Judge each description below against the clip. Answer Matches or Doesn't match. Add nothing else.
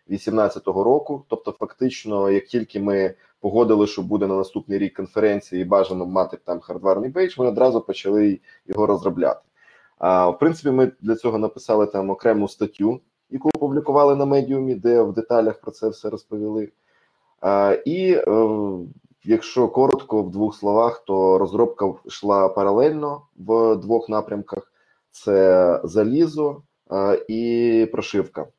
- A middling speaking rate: Matches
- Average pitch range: Matches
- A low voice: Matches